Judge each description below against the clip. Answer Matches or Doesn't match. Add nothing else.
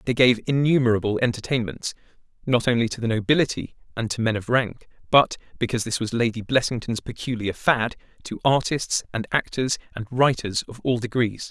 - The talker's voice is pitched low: Matches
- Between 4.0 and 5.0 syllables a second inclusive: Doesn't match